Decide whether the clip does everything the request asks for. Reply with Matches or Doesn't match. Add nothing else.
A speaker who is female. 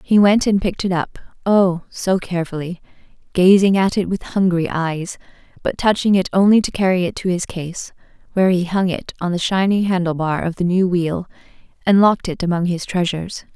Matches